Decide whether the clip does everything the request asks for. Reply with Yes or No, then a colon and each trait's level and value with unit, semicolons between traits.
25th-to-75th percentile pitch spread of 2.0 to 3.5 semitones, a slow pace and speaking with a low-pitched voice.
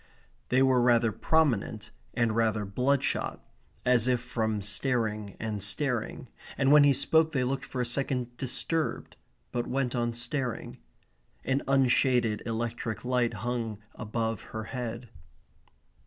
Yes: average, 2.7 semitones; slow, 130 wpm; low, 120 Hz